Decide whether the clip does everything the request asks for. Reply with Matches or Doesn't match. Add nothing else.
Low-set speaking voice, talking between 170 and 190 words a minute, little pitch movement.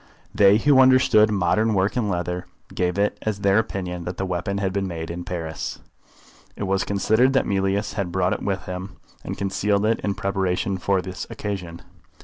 Matches